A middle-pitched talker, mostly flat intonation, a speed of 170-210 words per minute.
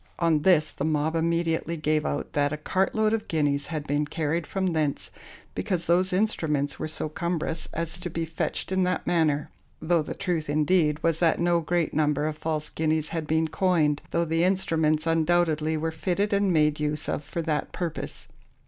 Yes: medium, 160 Hz; narrow, 2.2 semitones; average, 190 wpm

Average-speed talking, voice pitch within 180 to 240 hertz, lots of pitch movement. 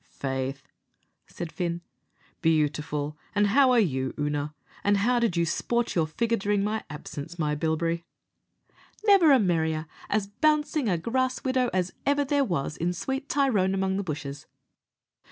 Yes: average, 155 wpm; medium, 185 Hz; wide, 7.5 semitones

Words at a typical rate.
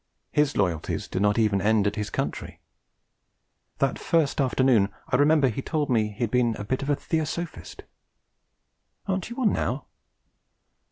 Yes: average, 160 wpm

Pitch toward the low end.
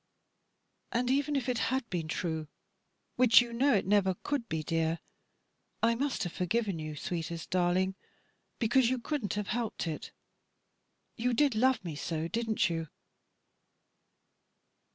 No: high, 215 Hz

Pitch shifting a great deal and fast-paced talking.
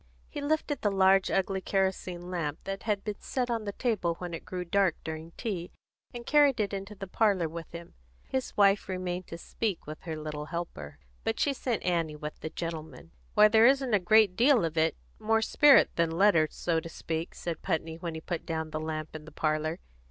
No: average, 4.6 semitones; fast, 210 wpm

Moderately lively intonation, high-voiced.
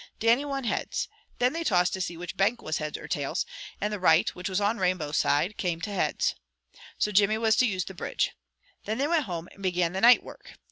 Yes: average, 4.3 semitones; high, 195 Hz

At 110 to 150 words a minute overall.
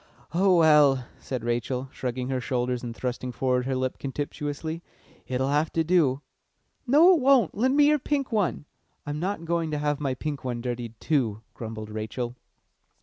No: average, 170 wpm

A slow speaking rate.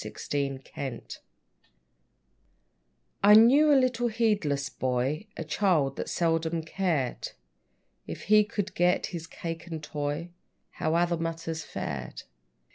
Yes: slow, 120 wpm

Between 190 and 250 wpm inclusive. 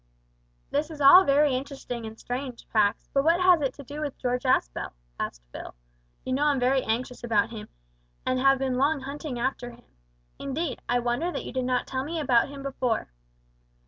Yes: average, 195 wpm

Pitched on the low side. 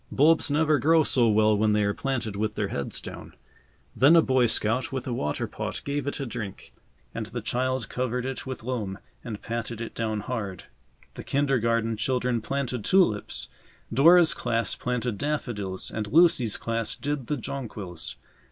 Yes: low, 120 Hz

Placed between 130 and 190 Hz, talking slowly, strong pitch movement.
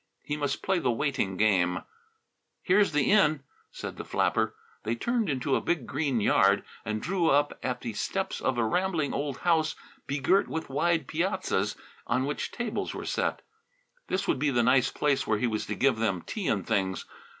No: medium, 140 Hz; average, 185 wpm; wide, 6.6 semitones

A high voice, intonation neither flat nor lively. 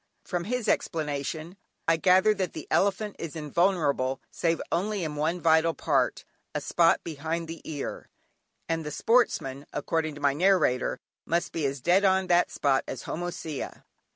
No: medium, 165 Hz; average, 3.5 semitones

